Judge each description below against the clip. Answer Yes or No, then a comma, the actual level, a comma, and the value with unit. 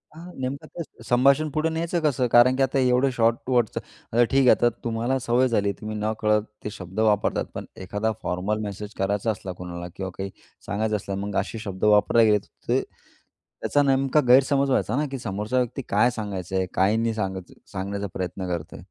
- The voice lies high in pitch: No, low, 110 Hz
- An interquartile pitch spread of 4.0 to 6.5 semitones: Yes, average, 4.3 semitones